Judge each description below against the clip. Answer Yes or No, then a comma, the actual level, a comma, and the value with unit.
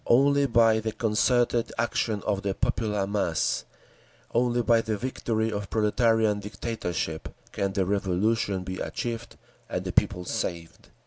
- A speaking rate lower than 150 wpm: Yes, slow, 135 wpm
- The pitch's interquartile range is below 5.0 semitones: Yes, average, 2.9 semitones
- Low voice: Yes, low, 110 Hz